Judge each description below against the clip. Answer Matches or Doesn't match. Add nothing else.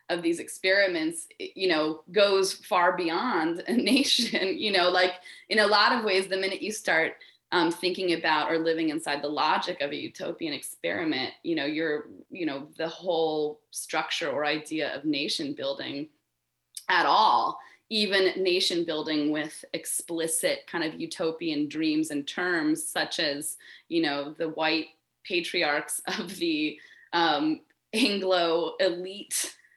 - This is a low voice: Doesn't match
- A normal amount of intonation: Doesn't match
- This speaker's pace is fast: Doesn't match